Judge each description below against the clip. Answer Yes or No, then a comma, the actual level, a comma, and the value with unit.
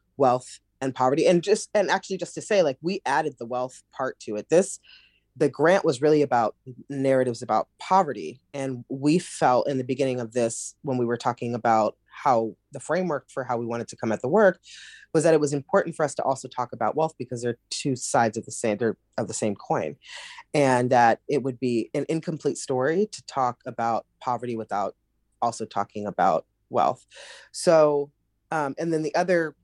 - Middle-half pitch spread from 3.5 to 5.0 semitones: Yes, average, 4.4 semitones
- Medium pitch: No, low, 130 Hz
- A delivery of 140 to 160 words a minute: No, average, 200 wpm